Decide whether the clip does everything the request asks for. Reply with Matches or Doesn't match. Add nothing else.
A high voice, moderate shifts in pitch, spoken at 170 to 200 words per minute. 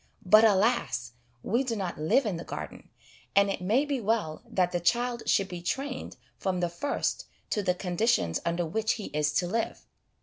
Matches